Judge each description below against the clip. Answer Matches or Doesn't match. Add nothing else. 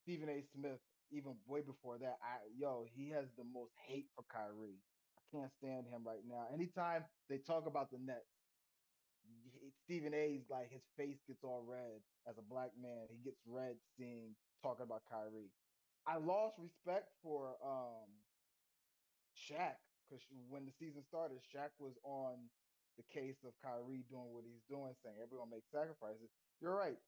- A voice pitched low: Matches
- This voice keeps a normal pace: Matches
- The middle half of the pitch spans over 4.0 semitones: Doesn't match